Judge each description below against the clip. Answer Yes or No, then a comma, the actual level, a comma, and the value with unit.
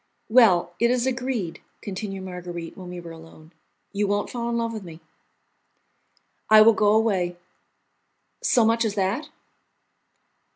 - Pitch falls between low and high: No, high, 205 Hz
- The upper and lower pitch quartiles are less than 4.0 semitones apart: No, average, 4.5 semitones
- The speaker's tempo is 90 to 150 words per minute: Yes, average, 140 wpm